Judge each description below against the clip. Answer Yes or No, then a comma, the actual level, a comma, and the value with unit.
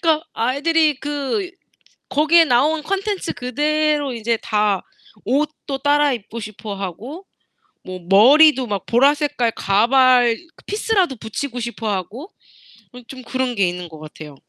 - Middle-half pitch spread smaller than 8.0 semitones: Yes, wide, 5.6 semitones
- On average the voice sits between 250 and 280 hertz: Yes, very high, 260 Hz